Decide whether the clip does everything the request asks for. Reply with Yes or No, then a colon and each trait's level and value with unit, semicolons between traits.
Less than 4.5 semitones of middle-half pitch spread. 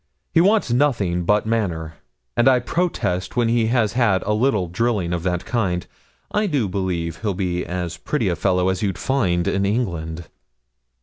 No: average, 5.2 semitones